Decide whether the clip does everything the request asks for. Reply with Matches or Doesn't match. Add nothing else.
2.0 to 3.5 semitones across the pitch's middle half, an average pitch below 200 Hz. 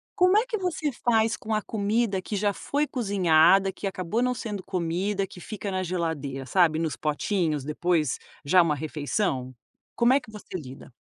Doesn't match